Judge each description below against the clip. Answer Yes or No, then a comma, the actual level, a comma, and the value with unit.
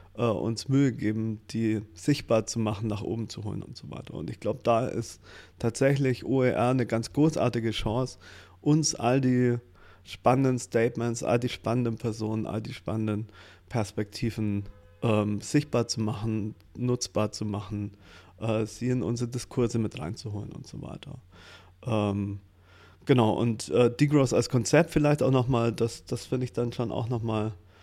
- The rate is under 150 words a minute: No, average, 155 wpm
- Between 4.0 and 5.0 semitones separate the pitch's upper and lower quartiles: No, average, 3.0 semitones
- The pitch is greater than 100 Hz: Yes, low, 115 Hz